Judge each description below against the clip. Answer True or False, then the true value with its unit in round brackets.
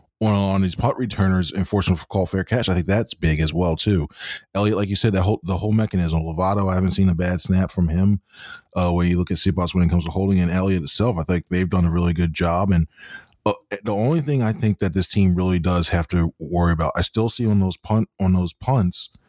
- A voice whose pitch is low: True (95 Hz)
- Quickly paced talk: True (250 wpm)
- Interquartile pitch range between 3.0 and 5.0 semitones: False (2.5 semitones)